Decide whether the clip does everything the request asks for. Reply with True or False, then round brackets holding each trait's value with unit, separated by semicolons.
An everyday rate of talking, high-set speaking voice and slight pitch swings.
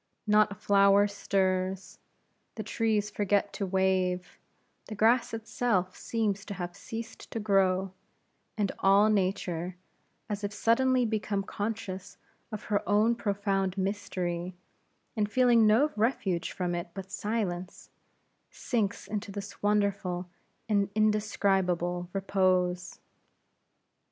False (115 wpm; 200 Hz; 2.3 semitones)